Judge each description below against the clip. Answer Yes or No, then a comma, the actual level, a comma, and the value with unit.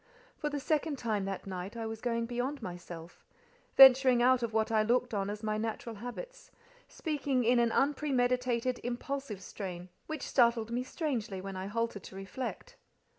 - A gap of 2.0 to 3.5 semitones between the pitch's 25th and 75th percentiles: No, average, 4.0 semitones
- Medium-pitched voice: No, high, 240 Hz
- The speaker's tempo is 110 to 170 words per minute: Yes, average, 160 wpm